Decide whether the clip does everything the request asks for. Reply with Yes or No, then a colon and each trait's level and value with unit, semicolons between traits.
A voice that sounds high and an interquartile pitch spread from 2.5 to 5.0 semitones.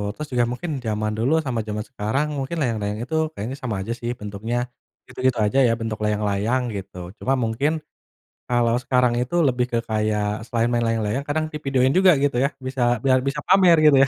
No: low, 120 Hz; average, 3.8 semitones